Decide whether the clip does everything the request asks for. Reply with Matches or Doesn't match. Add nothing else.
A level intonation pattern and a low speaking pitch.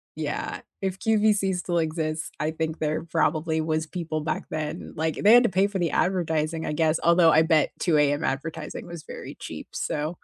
Doesn't match